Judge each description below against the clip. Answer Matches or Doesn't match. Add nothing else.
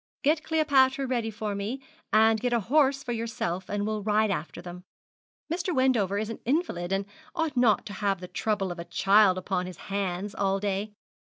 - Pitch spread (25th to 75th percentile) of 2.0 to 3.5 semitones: Doesn't match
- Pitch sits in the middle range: Doesn't match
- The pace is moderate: Matches